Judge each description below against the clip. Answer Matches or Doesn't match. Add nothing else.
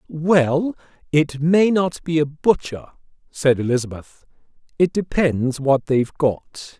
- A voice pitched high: Doesn't match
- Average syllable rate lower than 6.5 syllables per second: Matches